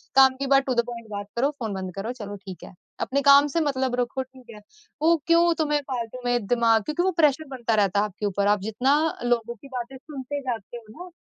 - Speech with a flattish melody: No, average, 4.1 semitones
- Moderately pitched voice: No, high, 245 Hz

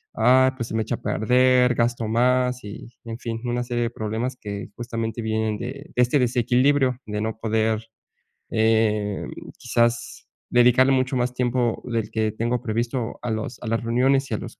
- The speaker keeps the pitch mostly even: Yes, narrow, 2.1 semitones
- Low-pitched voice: Yes, low, 120 Hz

